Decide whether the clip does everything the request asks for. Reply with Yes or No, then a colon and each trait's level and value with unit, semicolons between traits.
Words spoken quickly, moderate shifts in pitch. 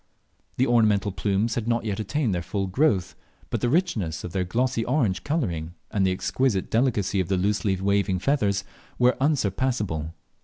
No: average, 165 wpm; average, 4.6 semitones